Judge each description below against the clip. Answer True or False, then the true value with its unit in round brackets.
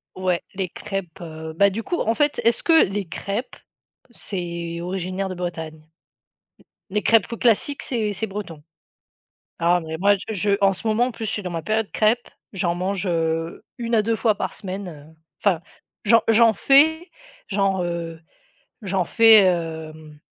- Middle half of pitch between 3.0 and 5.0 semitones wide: True (4.4 semitones)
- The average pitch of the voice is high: True (195 Hz)